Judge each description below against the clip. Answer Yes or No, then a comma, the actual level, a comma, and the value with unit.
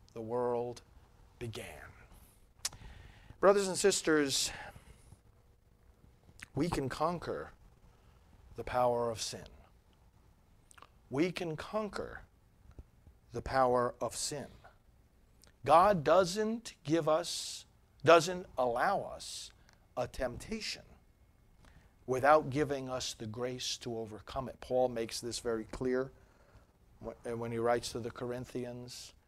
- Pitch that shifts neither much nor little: No, wide, 5.7 semitones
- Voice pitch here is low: Yes, low, 120 Hz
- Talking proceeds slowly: Yes, slow, 100 wpm